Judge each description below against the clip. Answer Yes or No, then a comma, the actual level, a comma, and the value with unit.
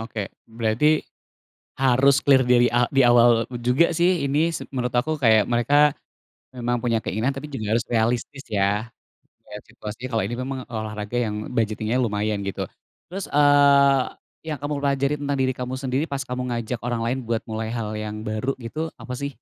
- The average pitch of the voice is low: Yes, low, 125 Hz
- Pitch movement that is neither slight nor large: Yes, average, 3.6 semitones